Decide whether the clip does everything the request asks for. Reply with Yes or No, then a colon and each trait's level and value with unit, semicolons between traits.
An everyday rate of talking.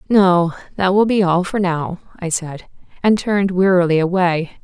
Yes: average, 170 wpm